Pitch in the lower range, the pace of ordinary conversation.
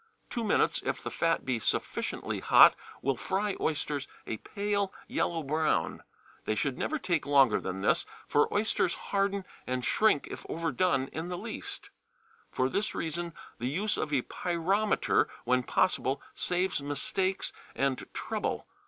No: medium, 165 Hz; average, 145 wpm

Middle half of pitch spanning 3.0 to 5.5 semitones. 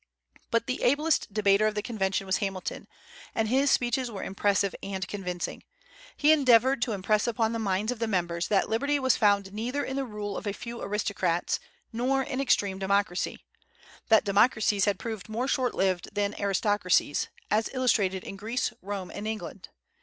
Yes: average, 3.4 semitones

